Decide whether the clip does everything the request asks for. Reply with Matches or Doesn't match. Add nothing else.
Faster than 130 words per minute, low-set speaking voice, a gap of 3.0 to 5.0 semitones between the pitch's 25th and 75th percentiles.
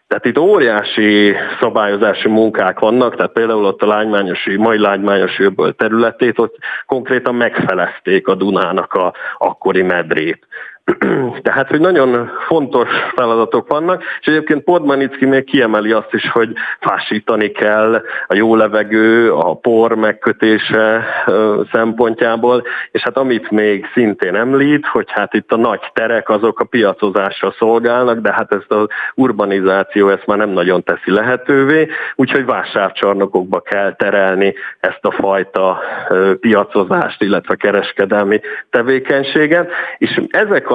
Doesn't match